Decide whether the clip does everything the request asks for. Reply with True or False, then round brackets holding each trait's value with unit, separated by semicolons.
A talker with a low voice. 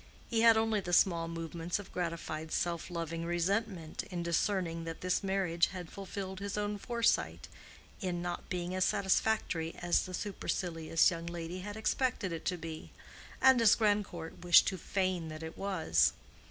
False (180 Hz)